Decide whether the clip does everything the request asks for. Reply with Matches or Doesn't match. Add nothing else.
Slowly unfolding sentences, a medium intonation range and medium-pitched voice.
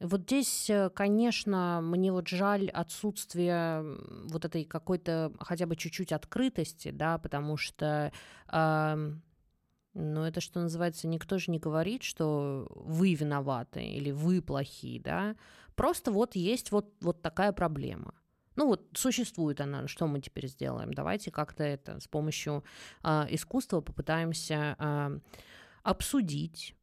Doesn't match